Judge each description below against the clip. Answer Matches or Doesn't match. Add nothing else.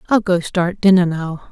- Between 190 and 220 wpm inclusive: Matches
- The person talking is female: Matches